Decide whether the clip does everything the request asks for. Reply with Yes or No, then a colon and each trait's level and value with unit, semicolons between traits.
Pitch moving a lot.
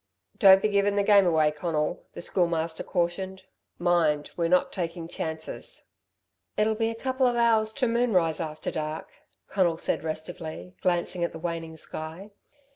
No: average, 3.9 semitones